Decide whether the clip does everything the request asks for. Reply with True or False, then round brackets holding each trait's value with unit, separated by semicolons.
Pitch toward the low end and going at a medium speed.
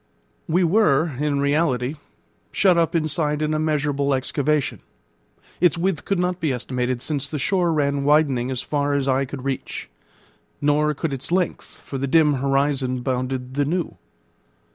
False (145 Hz; 155 wpm)